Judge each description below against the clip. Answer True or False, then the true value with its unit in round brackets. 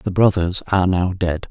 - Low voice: True (90 Hz)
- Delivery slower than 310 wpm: True (200 wpm)